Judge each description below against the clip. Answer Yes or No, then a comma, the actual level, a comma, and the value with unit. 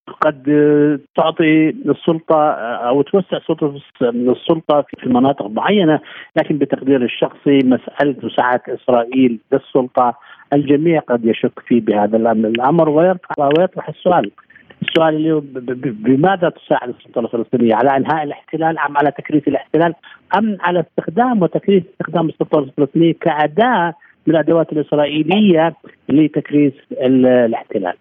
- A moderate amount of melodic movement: Yes, average, 4.0 semitones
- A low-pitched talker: No, medium, 150 Hz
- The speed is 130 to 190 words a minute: No, average, 110 wpm